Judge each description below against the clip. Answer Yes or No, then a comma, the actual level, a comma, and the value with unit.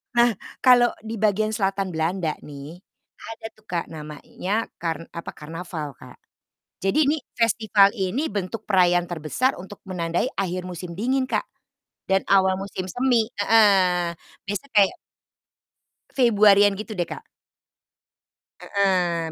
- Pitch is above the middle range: Yes, high, 195 Hz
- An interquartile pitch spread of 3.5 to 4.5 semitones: Yes, average, 3.8 semitones